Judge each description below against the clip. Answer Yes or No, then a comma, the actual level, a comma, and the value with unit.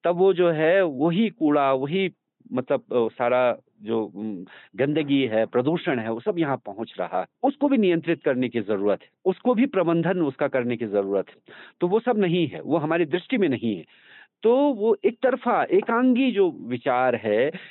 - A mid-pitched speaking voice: Yes, medium, 170 Hz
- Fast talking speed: No, average, 180 wpm